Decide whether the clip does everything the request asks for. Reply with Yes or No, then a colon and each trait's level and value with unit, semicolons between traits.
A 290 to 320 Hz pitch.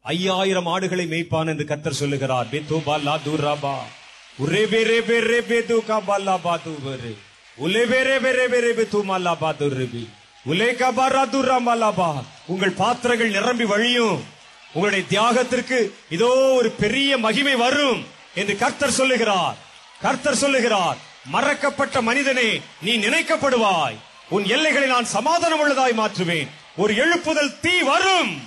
No: high, 220 Hz